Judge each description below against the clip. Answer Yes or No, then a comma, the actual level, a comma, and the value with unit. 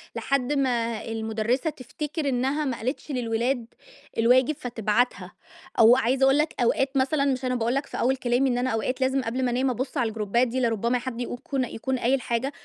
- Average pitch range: No, narrow, 2.3 semitones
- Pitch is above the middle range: Yes, very high, 250 Hz